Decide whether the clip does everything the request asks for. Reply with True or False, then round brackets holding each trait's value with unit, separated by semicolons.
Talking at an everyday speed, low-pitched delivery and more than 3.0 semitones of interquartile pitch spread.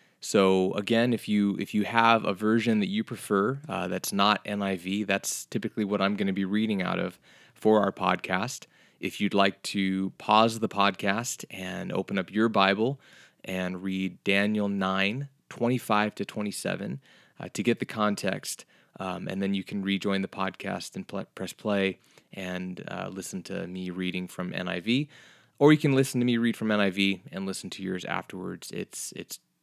False (180 wpm; 100 Hz; 2.7 semitones)